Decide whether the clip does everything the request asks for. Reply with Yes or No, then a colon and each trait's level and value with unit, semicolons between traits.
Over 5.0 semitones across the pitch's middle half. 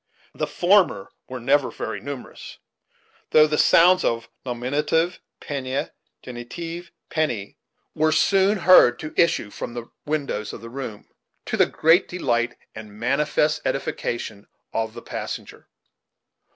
Yes: wide, 5.5 semitones